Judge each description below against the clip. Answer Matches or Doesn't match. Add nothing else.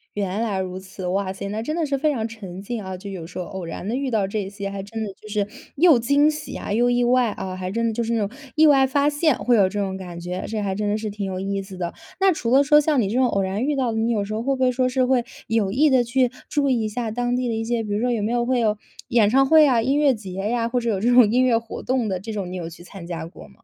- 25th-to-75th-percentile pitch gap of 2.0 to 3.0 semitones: Doesn't match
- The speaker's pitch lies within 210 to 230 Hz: Matches